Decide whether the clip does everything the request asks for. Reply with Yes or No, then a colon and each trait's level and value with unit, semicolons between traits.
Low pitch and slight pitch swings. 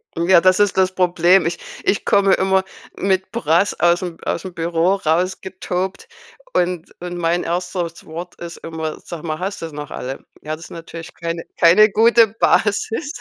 No: medium, 180 Hz; narrow, 2.3 semitones